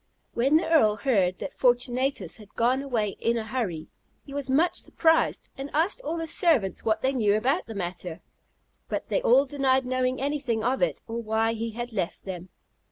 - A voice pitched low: No, high, 245 Hz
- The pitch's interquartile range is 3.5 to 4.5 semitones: Yes, average, 4.0 semitones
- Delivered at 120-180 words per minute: No, average, 190 wpm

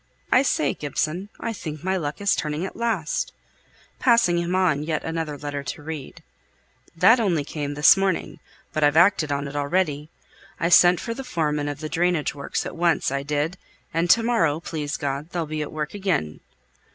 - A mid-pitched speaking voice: Yes, medium, 160 Hz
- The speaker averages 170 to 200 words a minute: Yes, average, 190 wpm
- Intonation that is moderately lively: Yes, average, 3.7 semitones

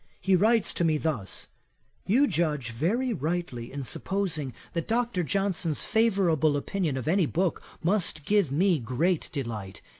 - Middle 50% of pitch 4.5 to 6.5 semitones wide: Yes, wide, 5.4 semitones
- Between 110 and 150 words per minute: Yes, average, 145 wpm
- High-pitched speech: No, medium, 170 Hz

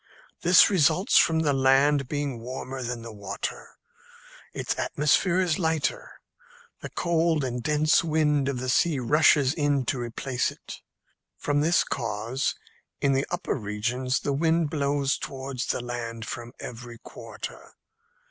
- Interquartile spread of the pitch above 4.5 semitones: No, average, 3.9 semitones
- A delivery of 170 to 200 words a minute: No, average, 140 wpm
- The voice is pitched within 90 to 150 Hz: Yes, medium, 140 Hz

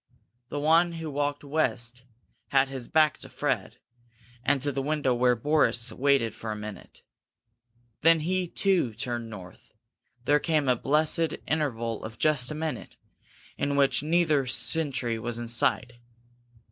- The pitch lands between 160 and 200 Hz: No, medium, 140 Hz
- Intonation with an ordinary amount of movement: Yes, average, 4.5 semitones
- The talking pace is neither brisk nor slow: Yes, average, 145 wpm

